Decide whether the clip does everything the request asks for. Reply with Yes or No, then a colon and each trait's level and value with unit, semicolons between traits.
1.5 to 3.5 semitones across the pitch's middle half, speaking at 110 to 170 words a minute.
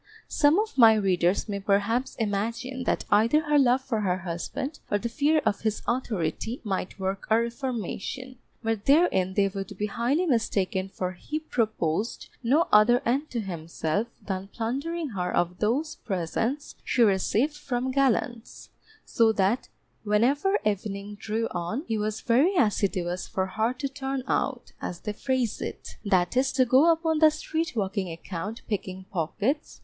No: average, 5.2 semitones; average, 160 wpm